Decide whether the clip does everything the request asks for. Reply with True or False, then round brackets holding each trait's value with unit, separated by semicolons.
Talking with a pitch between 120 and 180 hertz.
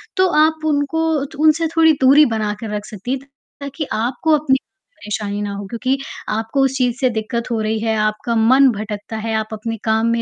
False (230 Hz)